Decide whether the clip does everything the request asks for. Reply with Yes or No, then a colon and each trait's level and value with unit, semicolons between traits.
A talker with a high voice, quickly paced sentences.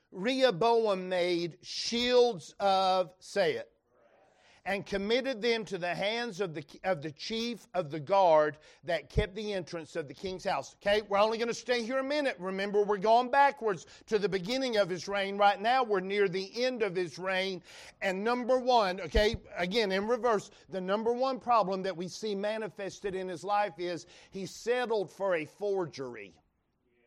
No: high, 200 Hz; average, 175 wpm